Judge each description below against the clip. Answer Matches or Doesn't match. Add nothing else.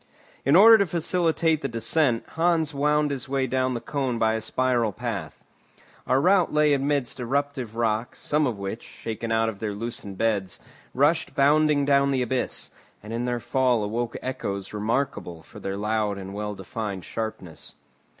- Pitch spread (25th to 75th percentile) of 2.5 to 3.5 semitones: Doesn't match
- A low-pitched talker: Matches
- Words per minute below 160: Doesn't match